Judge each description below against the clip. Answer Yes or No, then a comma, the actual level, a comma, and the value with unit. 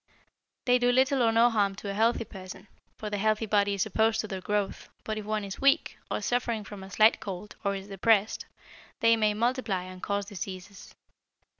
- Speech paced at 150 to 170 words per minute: No, average, 200 wpm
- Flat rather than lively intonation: Yes, narrow, 2.3 semitones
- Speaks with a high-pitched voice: Yes, high, 210 Hz